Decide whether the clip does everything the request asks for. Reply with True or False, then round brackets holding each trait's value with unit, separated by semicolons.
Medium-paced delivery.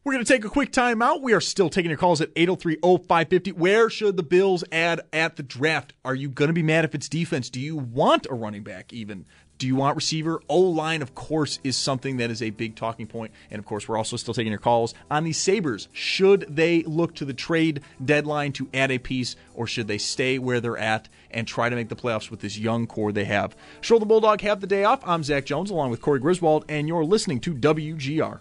False (245 wpm)